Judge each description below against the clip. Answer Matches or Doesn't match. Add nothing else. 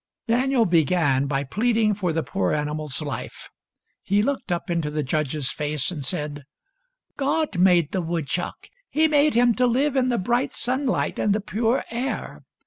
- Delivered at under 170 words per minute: Doesn't match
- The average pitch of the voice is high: Matches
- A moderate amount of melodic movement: Doesn't match